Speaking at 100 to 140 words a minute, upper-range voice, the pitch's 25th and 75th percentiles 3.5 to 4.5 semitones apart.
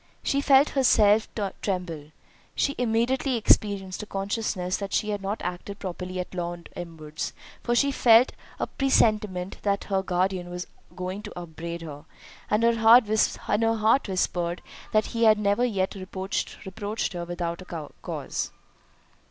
Yes: slow, 135 wpm; high, 195 Hz; average, 3.8 semitones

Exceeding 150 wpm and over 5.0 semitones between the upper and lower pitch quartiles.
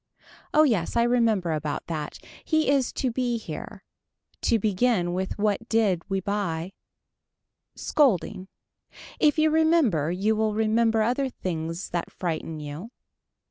No: slow, 135 wpm; wide, 5.6 semitones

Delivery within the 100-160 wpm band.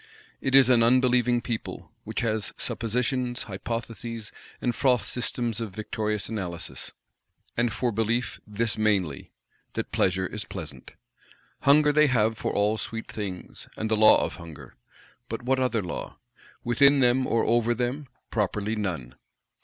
Yes: average, 145 wpm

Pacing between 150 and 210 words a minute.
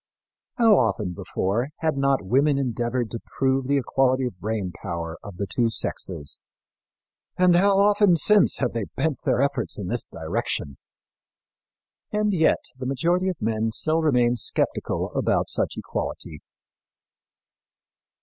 No: average, 140 wpm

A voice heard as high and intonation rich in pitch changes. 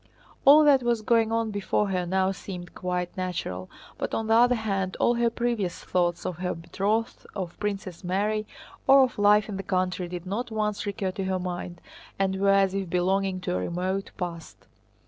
No: high, 195 Hz; average, 3.1 semitones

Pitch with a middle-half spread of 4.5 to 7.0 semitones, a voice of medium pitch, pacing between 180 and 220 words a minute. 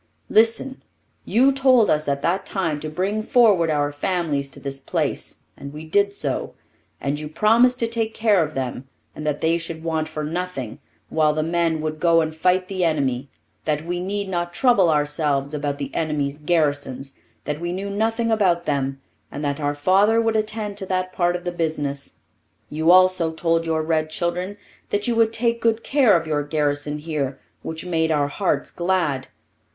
Yes: average, 4.8 semitones; medium, 165 Hz; average, 185 wpm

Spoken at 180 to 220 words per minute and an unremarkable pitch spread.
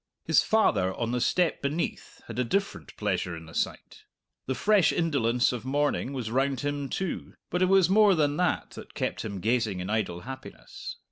No: average, 190 wpm; wide, 7.2 semitones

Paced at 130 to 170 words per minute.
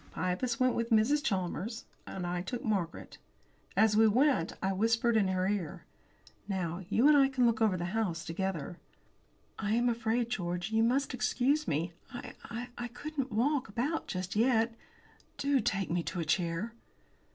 Yes: average, 165 wpm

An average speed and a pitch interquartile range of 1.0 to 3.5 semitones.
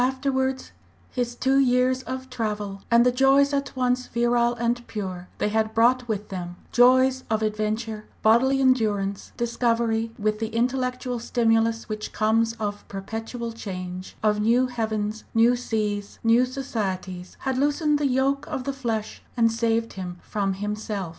Yes: average, 155 wpm; average, 3.0 semitones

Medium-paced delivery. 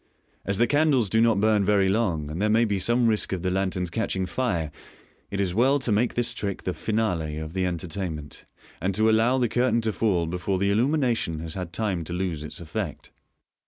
No: fast, 210 wpm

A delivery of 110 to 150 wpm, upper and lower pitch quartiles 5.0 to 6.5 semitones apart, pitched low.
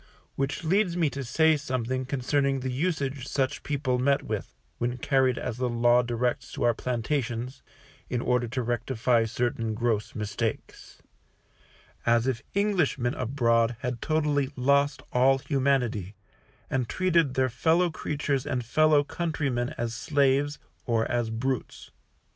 No: slow, 135 wpm; average, 3.0 semitones; low, 130 Hz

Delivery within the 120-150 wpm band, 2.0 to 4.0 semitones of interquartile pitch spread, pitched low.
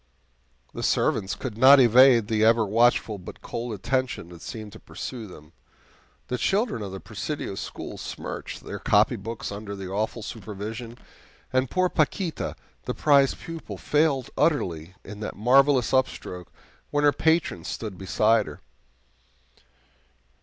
No: average, 140 wpm; average, 4.7 semitones; low, 115 Hz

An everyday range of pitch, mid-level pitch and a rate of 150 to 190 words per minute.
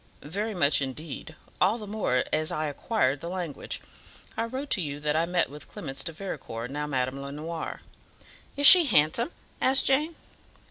No: wide, 6.9 semitones; medium, 160 Hz; average, 170 wpm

